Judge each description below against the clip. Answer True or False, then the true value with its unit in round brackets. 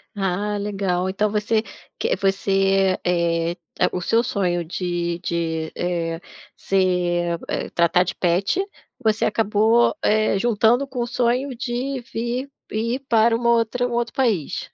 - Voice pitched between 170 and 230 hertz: True (200 Hz)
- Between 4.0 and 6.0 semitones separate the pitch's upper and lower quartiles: True (4.8 semitones)